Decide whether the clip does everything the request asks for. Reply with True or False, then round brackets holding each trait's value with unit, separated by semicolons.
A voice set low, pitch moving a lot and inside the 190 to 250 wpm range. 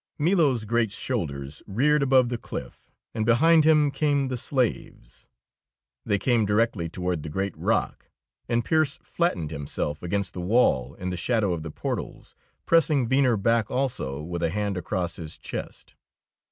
False (110 Hz; 7.1 semitones; 155 wpm)